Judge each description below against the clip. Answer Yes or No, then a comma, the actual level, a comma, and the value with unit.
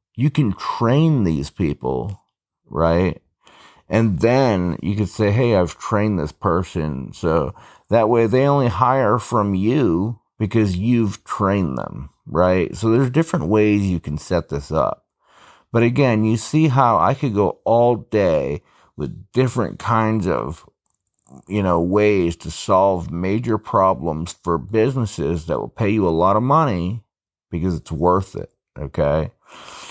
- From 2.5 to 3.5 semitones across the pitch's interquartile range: No, average, 4.7 semitones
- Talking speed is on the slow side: No, average, 150 wpm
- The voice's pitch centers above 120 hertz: No, low, 105 Hz